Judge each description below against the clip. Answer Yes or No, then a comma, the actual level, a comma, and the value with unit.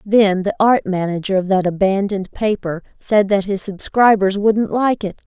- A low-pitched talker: No, high, 200 Hz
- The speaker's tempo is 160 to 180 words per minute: Yes, average, 170 wpm